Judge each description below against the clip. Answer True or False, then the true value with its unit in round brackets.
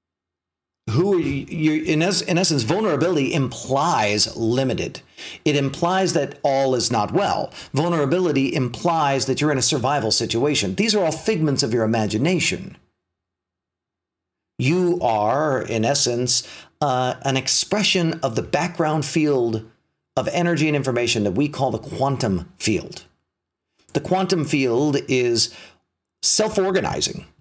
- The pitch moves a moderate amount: False (6.1 semitones)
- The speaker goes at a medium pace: False (125 wpm)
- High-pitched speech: False (135 Hz)